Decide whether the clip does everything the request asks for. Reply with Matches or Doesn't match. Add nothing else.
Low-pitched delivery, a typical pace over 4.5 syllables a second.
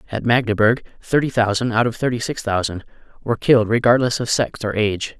Matches